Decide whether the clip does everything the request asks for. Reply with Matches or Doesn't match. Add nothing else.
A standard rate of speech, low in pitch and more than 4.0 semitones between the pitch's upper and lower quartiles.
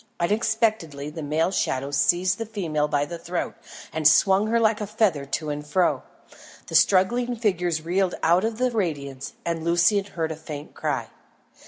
Doesn't match